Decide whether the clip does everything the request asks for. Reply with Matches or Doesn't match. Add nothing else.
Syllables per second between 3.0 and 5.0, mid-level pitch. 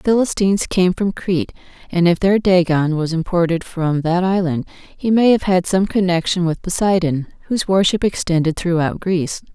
Doesn't match